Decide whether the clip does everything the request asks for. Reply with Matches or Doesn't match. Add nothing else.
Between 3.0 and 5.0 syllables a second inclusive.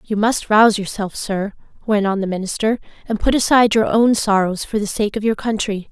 Doesn't match